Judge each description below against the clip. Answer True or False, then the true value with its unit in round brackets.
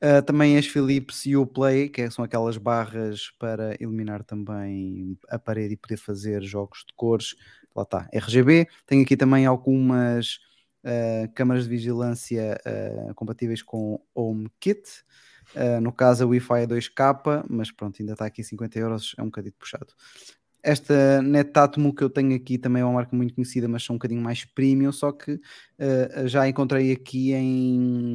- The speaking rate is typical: True (175 wpm)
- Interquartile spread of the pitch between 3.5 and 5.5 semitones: False (3.1 semitones)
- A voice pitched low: True (120 Hz)